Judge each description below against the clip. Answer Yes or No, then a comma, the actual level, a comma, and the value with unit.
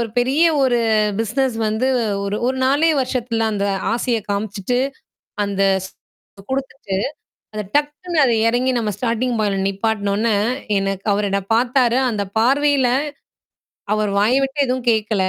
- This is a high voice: Yes, high, 230 Hz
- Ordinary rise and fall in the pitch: Yes, average, 3.8 semitones